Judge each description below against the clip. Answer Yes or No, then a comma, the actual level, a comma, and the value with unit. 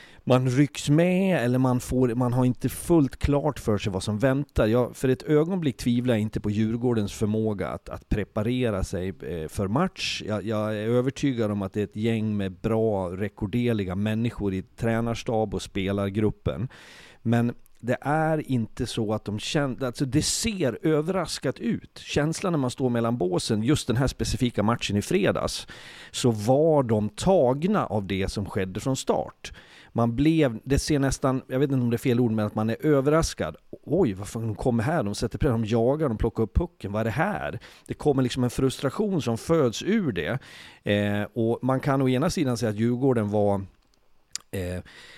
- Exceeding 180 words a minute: Yes, average, 190 wpm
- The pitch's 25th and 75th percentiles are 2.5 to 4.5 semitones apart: Yes, average, 4.1 semitones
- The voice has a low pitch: Yes, low, 120 Hz